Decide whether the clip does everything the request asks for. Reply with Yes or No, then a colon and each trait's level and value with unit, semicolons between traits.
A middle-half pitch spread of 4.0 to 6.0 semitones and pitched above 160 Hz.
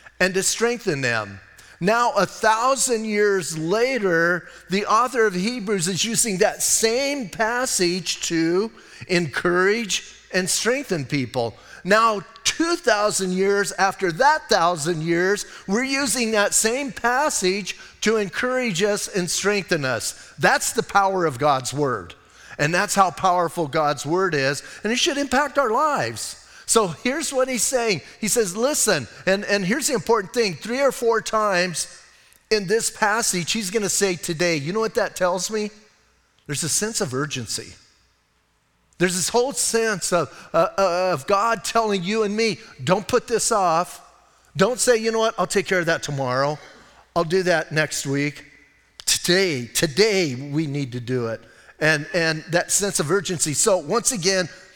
Yes: average, 5.2 semitones; high, 190 Hz